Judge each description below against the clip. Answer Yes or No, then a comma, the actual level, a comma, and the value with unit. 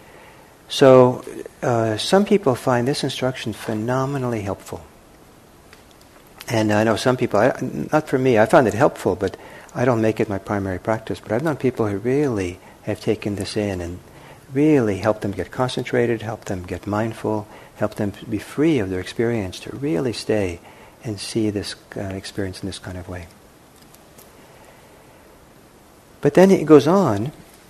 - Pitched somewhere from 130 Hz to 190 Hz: No, low, 110 Hz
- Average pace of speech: Yes, average, 165 wpm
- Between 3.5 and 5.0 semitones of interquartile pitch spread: Yes, average, 4.3 semitones